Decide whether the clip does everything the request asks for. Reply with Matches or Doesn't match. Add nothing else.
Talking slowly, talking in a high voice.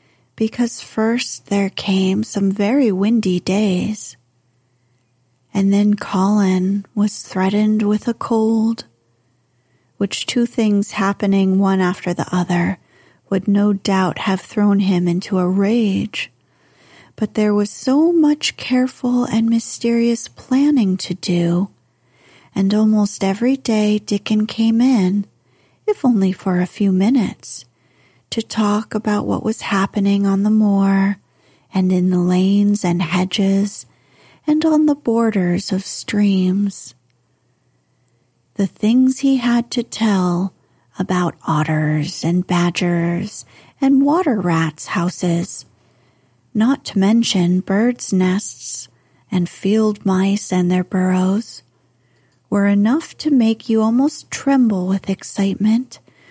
Matches